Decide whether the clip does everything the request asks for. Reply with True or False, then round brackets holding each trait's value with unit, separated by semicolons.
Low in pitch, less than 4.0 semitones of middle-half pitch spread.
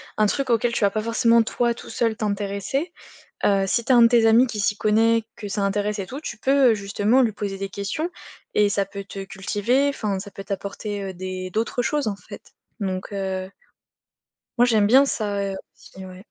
False (210 Hz; 2.9 semitones)